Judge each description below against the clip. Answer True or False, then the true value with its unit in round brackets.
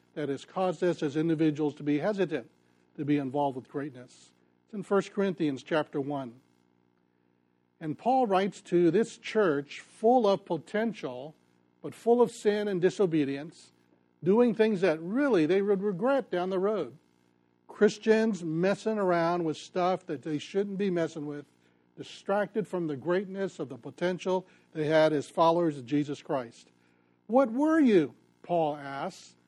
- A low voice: False (160 Hz)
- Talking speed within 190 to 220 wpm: False (155 wpm)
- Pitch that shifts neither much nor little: False (6.2 semitones)